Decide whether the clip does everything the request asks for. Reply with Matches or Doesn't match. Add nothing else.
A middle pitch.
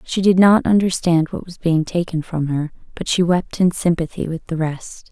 Matches